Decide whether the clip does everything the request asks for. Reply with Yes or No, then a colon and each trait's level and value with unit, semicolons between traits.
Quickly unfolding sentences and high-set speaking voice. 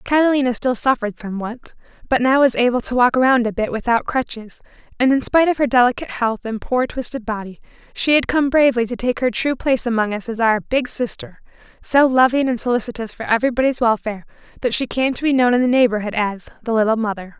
Yes: fast, 210 wpm; high, 240 Hz